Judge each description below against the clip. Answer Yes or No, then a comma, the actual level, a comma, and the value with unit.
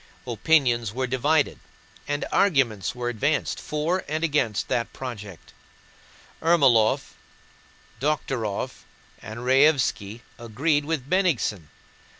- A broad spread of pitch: No, average, 4.8 semitones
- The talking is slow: Yes, slow, 95 wpm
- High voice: No, low, 130 Hz